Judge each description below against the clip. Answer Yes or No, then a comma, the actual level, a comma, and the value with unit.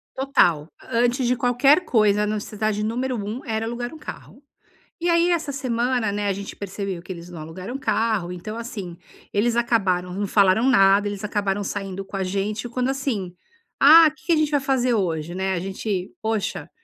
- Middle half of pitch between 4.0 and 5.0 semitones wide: Yes, average, 4.3 semitones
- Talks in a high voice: Yes, high, 215 Hz